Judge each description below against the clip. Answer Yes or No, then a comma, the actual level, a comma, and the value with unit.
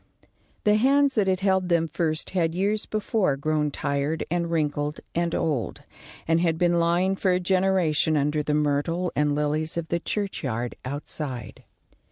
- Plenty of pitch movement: No, average, 3.8 semitones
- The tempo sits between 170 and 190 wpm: No, average, 160 wpm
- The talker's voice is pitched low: No, medium, 165 Hz